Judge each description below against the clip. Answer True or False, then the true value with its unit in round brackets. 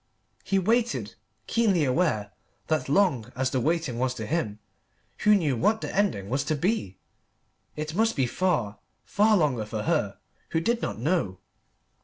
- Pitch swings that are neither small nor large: False (7.9 semitones)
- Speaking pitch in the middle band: True (155 Hz)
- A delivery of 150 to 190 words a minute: True (160 wpm)